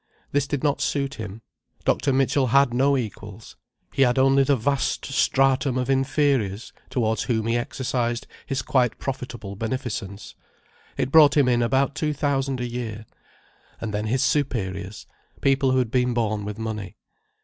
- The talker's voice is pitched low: Yes, low, 125 Hz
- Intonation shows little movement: No, average, 3.4 semitones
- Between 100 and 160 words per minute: Yes, average, 155 wpm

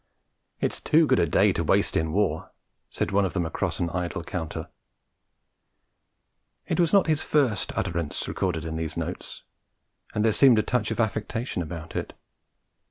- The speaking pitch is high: No, very low, 95 Hz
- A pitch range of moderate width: No, wide, 6.3 semitones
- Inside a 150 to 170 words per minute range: Yes, average, 165 wpm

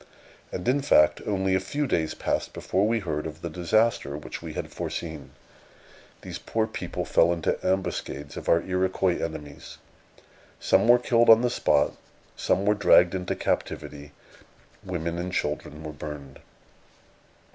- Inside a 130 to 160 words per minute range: Yes, average, 150 wpm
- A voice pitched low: Yes, very low, 90 Hz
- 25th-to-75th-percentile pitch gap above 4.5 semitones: Yes, average, 5.2 semitones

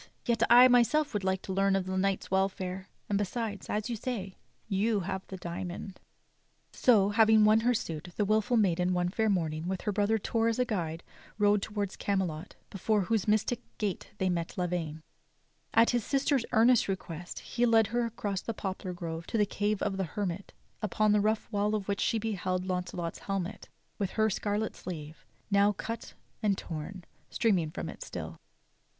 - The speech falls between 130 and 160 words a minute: No, average, 180 wpm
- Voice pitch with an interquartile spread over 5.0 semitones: No, average, 3.0 semitones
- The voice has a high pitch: Yes, high, 200 Hz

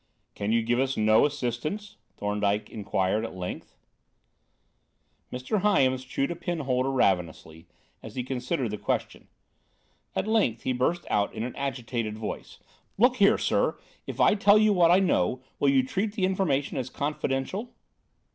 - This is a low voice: Yes, low, 130 Hz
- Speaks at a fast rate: No, average, 155 wpm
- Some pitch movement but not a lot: No, wide, 7.8 semitones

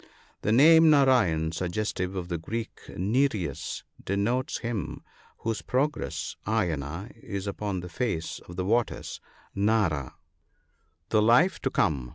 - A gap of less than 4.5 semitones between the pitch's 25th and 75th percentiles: No, average, 5.3 semitones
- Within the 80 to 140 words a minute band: Yes, slow, 135 wpm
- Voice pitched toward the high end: No, low, 105 Hz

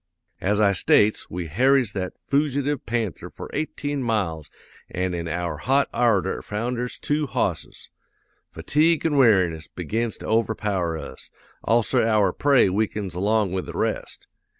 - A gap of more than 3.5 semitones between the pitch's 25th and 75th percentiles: Yes, wide, 5.6 semitones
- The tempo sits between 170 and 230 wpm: No, average, 140 wpm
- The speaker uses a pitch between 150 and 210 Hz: No, low, 110 Hz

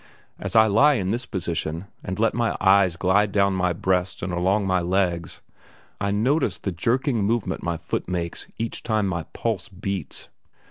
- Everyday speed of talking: Yes, average, 175 wpm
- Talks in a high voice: No, very low, 95 Hz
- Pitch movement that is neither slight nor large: Yes, average, 3.4 semitones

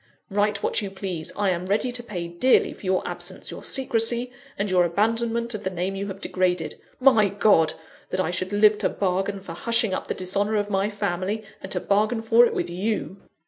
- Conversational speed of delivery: No, fast, 210 wpm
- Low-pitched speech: No, high, 200 Hz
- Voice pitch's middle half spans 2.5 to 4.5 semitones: Yes, average, 2.9 semitones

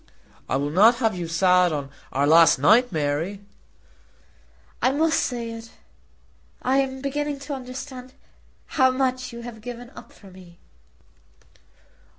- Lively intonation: Yes, wide, 6.6 semitones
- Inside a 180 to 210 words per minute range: No, average, 140 wpm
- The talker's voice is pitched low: No, high, 235 Hz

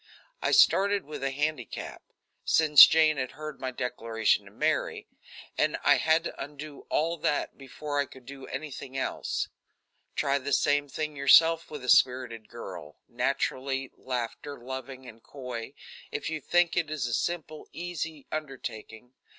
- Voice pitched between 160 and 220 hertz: No, medium, 140 Hz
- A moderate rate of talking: Yes, average, 150 wpm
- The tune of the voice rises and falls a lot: No, average, 3.4 semitones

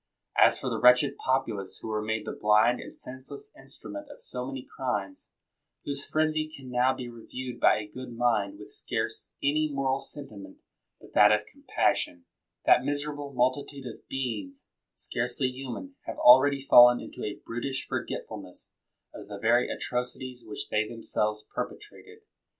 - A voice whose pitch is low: Yes, low, 125 Hz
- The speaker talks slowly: No, average, 155 wpm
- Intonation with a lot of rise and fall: No, average, 3.7 semitones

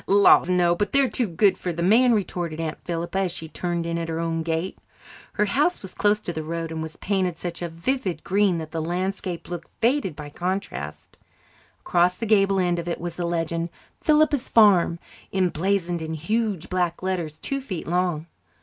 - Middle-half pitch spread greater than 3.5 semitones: No, average, 3.0 semitones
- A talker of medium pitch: Yes, medium, 175 Hz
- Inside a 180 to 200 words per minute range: Yes, average, 195 wpm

